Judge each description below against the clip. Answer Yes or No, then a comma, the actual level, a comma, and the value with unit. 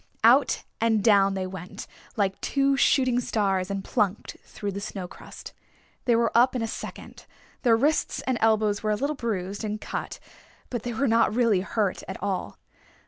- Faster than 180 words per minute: No, average, 175 wpm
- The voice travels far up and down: No, average, 3.2 semitones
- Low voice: No, high, 215 Hz